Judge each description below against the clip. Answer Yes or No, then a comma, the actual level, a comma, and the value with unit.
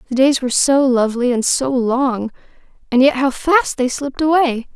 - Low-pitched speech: No, very high, 260 Hz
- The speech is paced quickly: No, average, 190 wpm